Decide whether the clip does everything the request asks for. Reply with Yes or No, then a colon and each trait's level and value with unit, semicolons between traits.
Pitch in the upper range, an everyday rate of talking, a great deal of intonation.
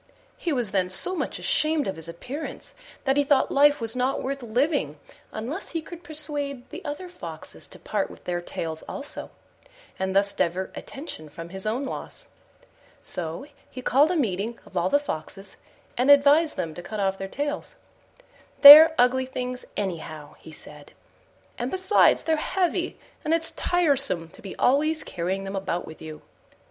Yes: very high, 250 Hz; average, 170 wpm; wide, 7.9 semitones